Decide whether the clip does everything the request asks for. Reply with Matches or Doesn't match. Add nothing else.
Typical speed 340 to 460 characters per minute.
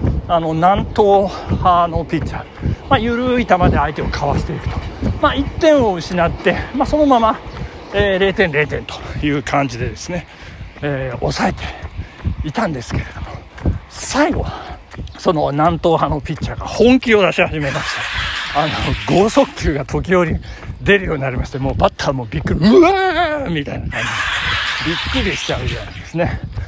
Doesn't match